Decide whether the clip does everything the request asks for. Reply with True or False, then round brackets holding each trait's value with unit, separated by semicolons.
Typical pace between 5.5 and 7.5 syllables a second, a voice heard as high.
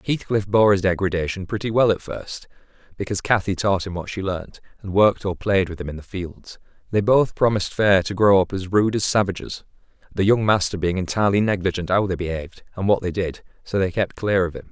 False (5.9 syllables/s; 95 Hz)